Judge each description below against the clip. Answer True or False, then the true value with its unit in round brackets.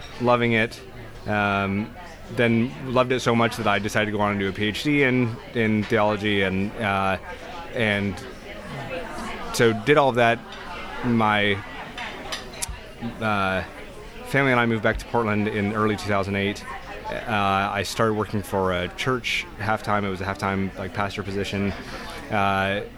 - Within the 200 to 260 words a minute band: False (155 wpm)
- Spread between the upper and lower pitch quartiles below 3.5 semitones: True (2.8 semitones)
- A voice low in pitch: True (105 Hz)